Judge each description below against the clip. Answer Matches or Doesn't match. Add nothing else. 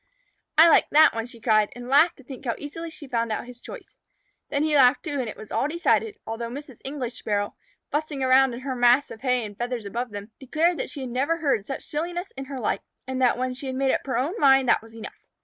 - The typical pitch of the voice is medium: Doesn't match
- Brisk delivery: Matches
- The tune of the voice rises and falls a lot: Doesn't match